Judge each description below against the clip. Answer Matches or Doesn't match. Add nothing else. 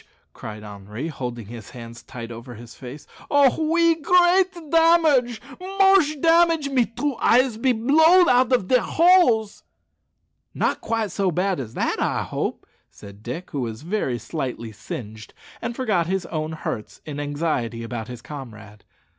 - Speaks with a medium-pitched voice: Matches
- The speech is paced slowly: Doesn't match